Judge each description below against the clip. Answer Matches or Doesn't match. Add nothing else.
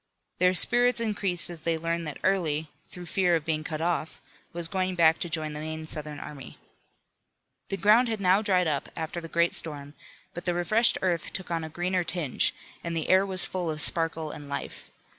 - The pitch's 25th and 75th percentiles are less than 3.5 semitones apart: Matches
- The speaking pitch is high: Doesn't match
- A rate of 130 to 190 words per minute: Doesn't match